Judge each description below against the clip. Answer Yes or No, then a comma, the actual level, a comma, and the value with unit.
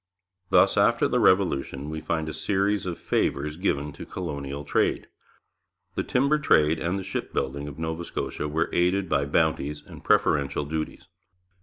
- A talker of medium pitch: No, very low, 80 Hz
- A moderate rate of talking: Yes, average, 155 wpm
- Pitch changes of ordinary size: Yes, average, 3.9 semitones